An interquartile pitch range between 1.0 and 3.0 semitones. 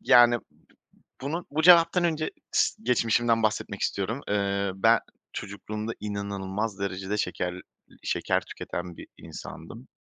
No: average, 3.5 semitones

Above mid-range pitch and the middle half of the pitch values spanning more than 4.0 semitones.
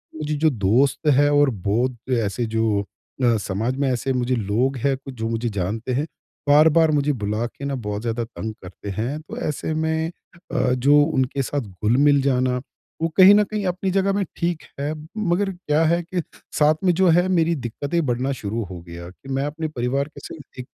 No: low, 135 Hz; average, 4.9 semitones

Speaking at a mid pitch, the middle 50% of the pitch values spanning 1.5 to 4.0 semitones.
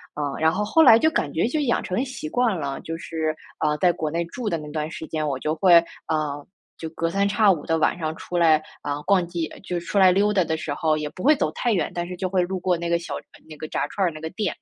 Yes: medium, 170 Hz; average, 3.7 semitones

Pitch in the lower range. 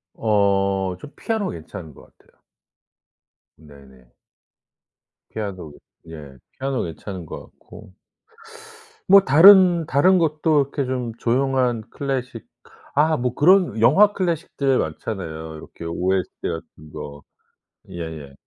Yes: low, 115 Hz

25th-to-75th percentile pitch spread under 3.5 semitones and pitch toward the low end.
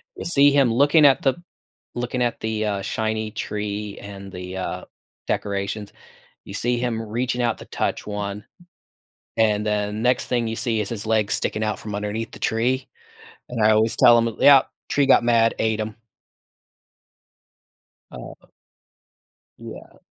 Yes: average, 2.7 semitones; low, 110 Hz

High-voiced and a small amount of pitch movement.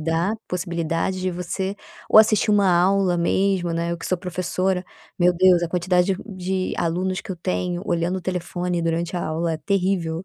No: medium, 180 Hz; narrow, 1.7 semitones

